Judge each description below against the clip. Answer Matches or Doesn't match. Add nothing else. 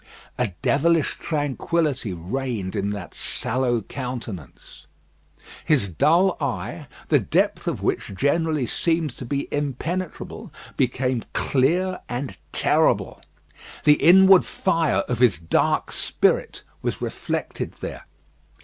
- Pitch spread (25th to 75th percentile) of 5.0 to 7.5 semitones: Matches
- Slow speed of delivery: Matches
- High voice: Doesn't match